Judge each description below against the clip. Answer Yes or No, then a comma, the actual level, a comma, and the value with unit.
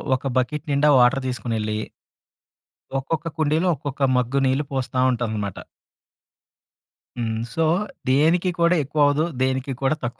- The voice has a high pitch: No, low, 135 Hz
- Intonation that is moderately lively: Yes, average, 3.5 semitones